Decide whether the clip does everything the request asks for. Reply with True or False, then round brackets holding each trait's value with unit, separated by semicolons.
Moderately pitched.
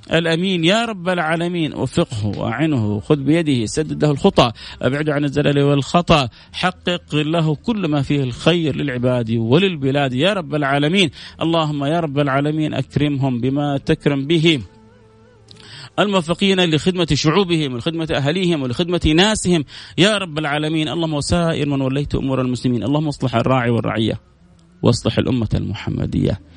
True (145 Hz)